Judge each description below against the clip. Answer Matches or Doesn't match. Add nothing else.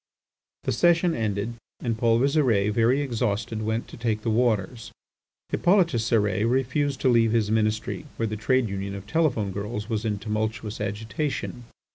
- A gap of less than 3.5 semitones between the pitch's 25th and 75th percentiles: Matches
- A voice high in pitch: Doesn't match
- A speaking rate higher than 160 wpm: Doesn't match